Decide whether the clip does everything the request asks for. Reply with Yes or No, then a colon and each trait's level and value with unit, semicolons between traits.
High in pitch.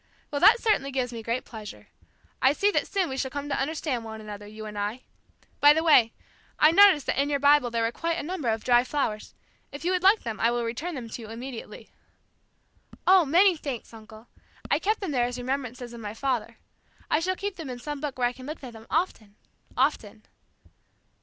Yes: very high, 260 Hz